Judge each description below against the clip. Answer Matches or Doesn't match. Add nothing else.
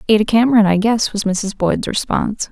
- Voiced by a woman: Matches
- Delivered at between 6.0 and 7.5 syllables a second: Doesn't match